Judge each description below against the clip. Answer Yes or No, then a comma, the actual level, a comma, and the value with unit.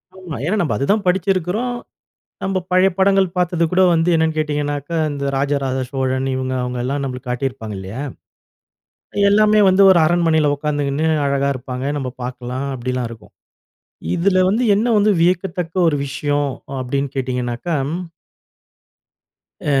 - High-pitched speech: No, medium, 145 Hz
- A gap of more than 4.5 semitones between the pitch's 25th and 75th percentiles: Yes, wide, 5.6 semitones